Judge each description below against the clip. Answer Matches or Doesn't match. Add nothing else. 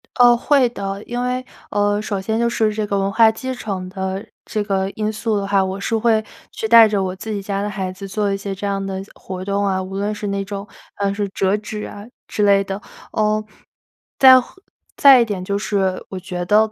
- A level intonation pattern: Matches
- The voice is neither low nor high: Doesn't match